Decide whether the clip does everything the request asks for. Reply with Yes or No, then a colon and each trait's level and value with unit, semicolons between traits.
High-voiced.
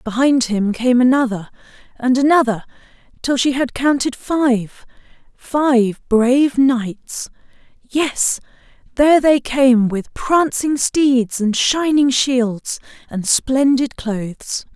Yes: very high, 255 Hz